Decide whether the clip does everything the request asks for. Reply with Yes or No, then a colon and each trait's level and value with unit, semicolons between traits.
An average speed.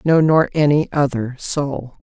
Yes: average, 150 wpm